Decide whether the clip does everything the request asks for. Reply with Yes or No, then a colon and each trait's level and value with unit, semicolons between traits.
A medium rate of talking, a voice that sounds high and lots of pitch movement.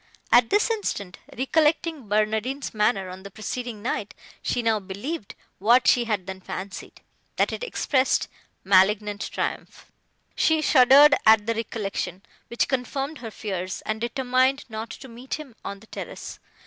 No: average, 150 wpm; high, 230 Hz; average, 4.5 semitones